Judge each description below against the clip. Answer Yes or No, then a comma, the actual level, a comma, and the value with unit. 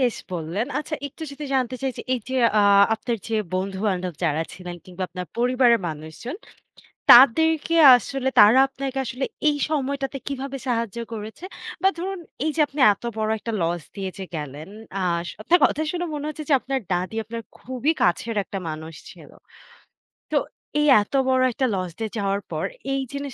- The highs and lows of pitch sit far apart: Yes, wide, 6.3 semitones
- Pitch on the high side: Yes, high, 240 Hz